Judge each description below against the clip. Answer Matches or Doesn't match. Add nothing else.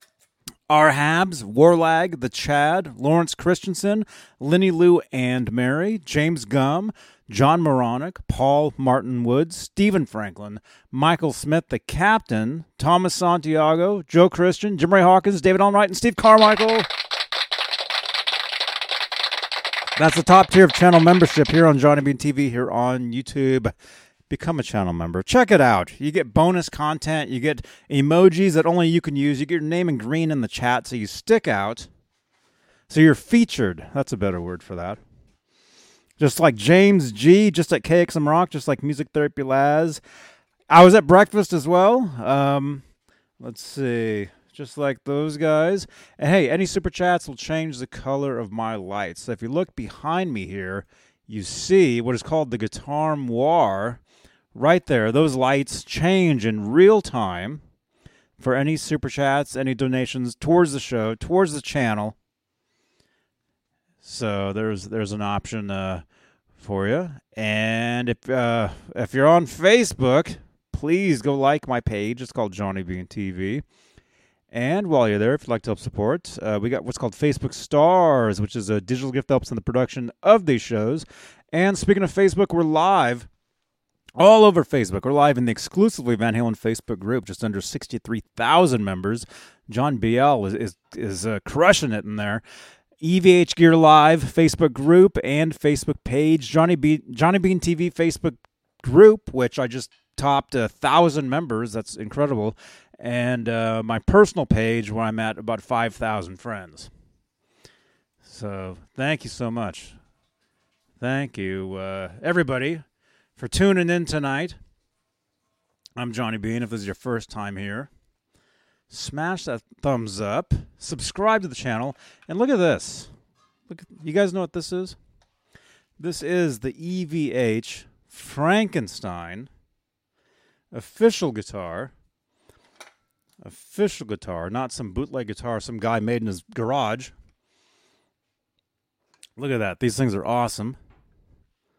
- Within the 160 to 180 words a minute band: Doesn't match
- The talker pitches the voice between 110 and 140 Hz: Matches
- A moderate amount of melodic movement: Doesn't match